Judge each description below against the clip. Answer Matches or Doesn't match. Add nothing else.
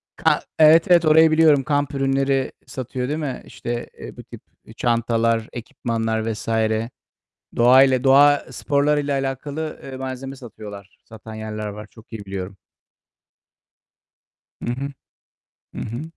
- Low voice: Matches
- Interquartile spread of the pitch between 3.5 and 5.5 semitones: Matches